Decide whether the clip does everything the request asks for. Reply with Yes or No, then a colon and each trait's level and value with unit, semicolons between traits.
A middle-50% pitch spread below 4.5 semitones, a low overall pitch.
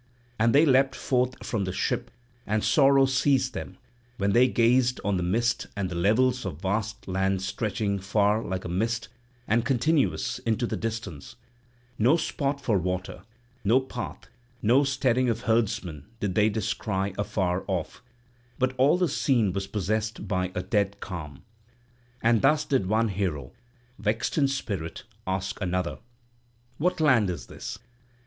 No: average, 5.0 semitones; low, 110 Hz